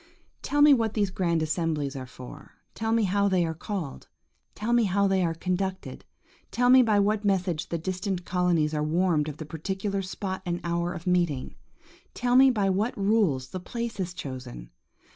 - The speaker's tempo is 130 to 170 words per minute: No, average, 185 wpm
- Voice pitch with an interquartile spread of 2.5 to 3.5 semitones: No, average, 4.0 semitones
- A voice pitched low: No, medium, 185 Hz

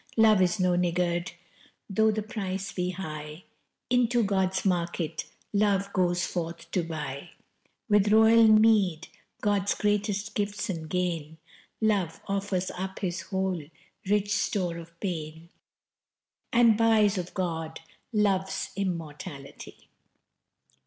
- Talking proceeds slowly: Yes, slow, 115 wpm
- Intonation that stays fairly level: No, average, 3.3 semitones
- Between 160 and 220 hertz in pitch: Yes, high, 190 Hz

